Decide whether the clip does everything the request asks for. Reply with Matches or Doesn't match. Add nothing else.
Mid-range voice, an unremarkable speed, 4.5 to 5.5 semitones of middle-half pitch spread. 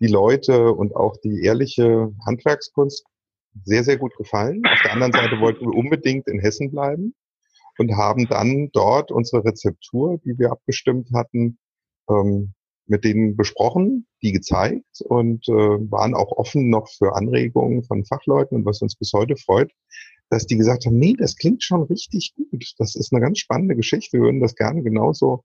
Doesn't match